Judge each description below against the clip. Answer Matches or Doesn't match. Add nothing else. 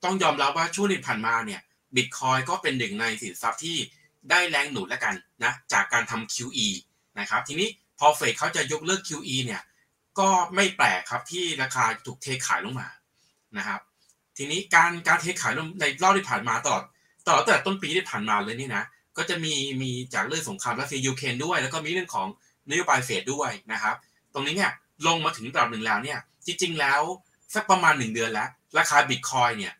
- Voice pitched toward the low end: Doesn't match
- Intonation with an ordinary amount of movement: Doesn't match